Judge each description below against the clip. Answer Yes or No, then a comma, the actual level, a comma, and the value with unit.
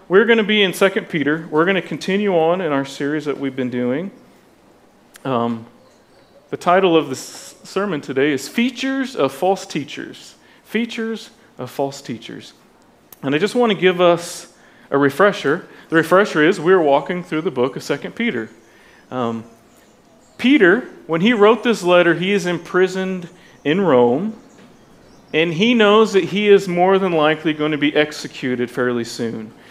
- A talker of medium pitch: Yes, medium, 170 Hz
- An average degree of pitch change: No, wide, 6.2 semitones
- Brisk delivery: No, average, 165 wpm